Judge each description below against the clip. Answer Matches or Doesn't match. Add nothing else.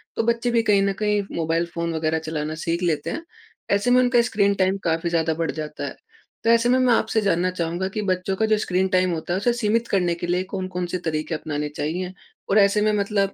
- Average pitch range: Matches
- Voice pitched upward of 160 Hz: Matches